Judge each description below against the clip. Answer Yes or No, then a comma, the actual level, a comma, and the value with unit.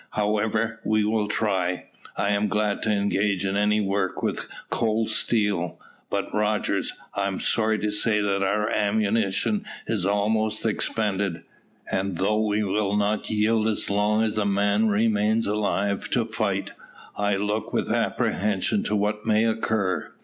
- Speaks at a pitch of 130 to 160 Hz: No, low, 105 Hz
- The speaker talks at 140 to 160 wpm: Yes, average, 150 wpm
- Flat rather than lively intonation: Yes, narrow, 1.3 semitones